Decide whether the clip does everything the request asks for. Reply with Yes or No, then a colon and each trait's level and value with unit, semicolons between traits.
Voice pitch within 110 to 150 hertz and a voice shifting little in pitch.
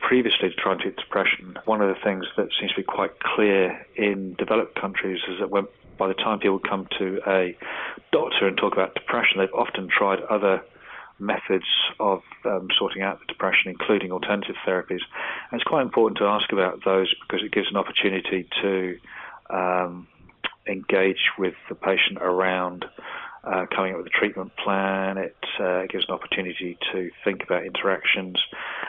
No: very low, 95 Hz; narrow, 1.3 semitones